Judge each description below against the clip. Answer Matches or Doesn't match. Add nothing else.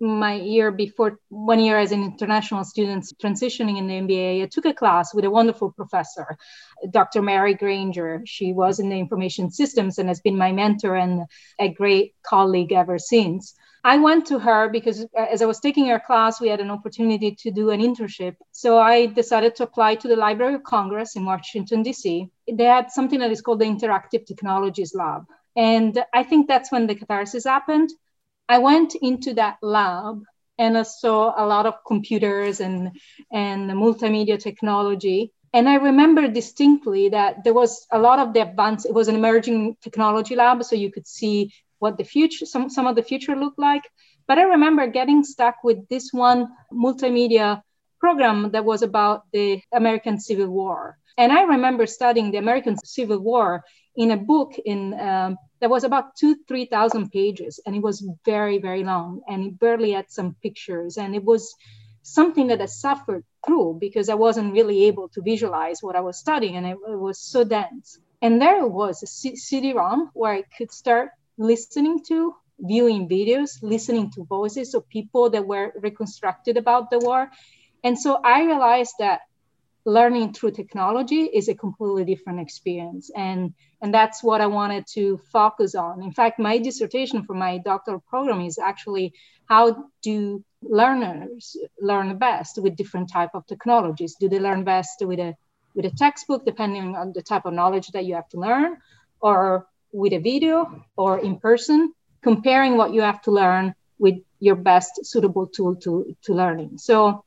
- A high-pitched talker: Matches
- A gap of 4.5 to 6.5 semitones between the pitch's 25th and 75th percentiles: Doesn't match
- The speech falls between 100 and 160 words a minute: Doesn't match